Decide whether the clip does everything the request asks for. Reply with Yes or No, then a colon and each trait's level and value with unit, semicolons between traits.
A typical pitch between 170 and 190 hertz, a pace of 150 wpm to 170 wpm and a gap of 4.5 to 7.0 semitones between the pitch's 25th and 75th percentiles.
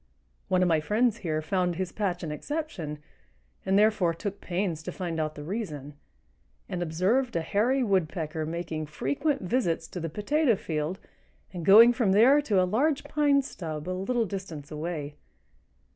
Yes: medium, 185 Hz; average, 165 wpm; wide, 5.6 semitones